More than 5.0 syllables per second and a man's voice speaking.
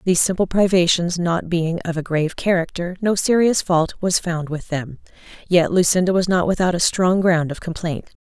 No: 5.2 syllables/s; female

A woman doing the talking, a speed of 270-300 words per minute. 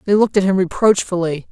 No: female; average, 200 wpm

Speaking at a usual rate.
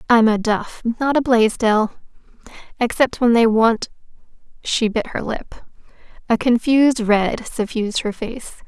No: slow, 130 wpm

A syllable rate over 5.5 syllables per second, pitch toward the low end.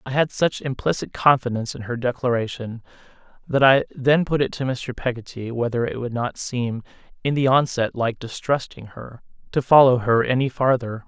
No: 5.1 syllables/s; low, 125 Hz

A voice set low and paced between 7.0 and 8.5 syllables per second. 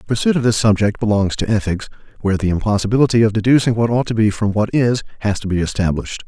Yes: low, 110 Hz; 7.1 syllables/s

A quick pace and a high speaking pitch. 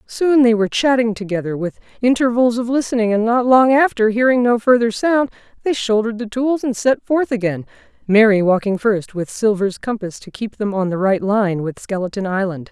No: average, 195 wpm; high, 220 Hz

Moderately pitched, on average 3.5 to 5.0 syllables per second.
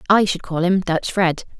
Yes: medium, 180 Hz; 4.9 syllables/s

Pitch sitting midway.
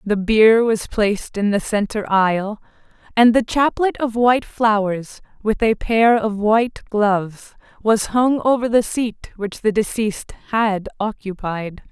No: high, 215 Hz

